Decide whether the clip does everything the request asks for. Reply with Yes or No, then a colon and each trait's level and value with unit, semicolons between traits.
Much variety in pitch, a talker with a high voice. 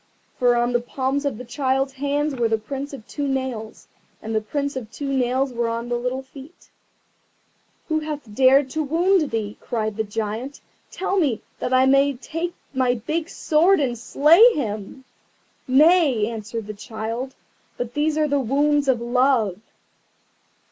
No: average, 3.7 semitones; very high, 260 Hz